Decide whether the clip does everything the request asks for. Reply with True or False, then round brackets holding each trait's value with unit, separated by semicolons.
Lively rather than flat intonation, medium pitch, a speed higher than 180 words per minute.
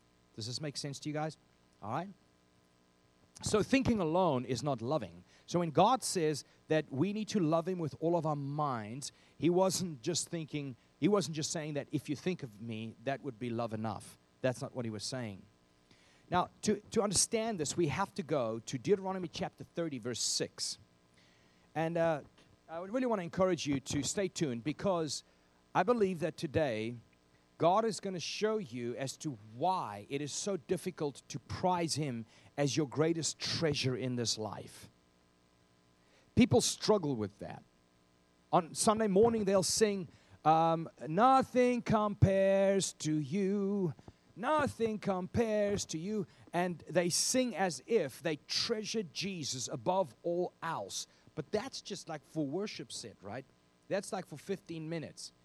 False (8.2 semitones; 155 Hz; 165 wpm)